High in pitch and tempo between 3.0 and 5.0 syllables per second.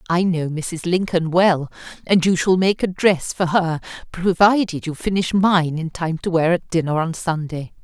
No: medium, 170 Hz; 4.5 syllables/s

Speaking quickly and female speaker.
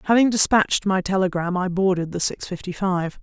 No: average, 185 wpm; female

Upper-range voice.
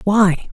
Yes: high, 195 Hz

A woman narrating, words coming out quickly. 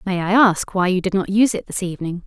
Yes: female; fast, 290 wpm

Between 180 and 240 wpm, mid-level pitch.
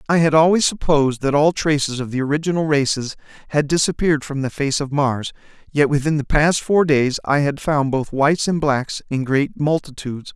Yes: average, 195 wpm; medium, 145 Hz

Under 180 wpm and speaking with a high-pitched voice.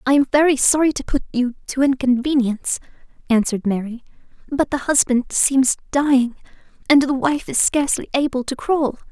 Yes: average, 160 wpm; very high, 265 Hz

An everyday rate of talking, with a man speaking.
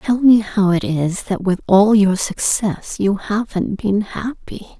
No: average, 175 wpm; female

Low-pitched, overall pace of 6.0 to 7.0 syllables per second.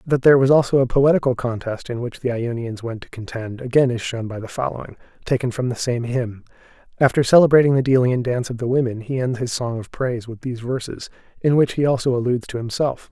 Yes: low, 125 Hz; 6.2 syllables/s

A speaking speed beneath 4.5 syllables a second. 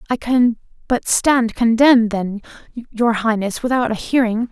Yes: 4.3 syllables/s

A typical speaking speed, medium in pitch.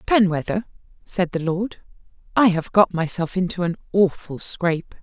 Yes: average, 145 wpm; medium, 180 Hz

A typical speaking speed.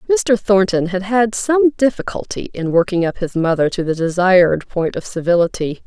Yes: average, 175 wpm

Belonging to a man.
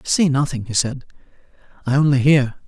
Yes: male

